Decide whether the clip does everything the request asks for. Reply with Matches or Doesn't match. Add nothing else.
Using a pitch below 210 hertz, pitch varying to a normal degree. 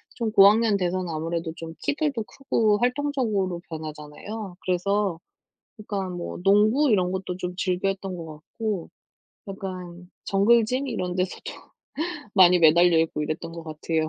Matches